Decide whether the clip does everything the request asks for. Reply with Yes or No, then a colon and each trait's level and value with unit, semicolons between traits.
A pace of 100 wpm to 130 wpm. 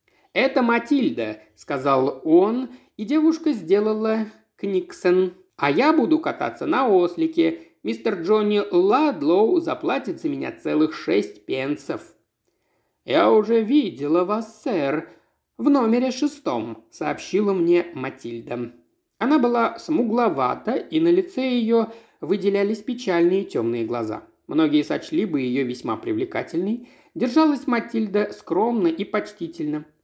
Yes: slow, 110 wpm